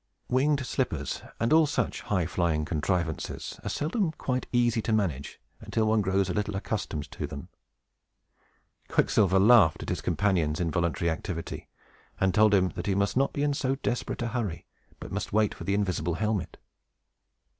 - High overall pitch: No, low, 100 Hz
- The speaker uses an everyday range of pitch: No, wide, 5.7 semitones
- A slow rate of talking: No, average, 165 wpm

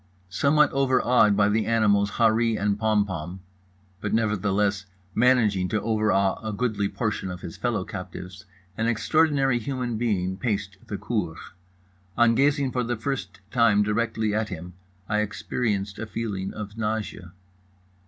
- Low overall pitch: Yes, low, 105 Hz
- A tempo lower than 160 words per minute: Yes, average, 140 wpm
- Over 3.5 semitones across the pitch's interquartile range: No, average, 3.0 semitones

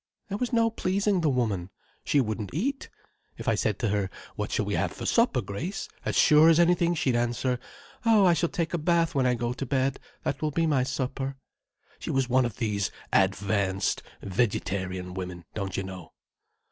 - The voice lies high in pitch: No, low, 130 Hz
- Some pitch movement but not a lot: No, wide, 8.7 semitones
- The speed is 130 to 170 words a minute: No, average, 190 wpm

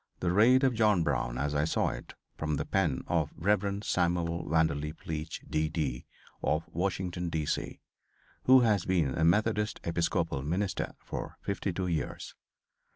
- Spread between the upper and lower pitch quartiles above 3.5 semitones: Yes, average, 4.2 semitones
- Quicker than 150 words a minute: Yes, average, 170 wpm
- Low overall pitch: Yes, very low, 85 Hz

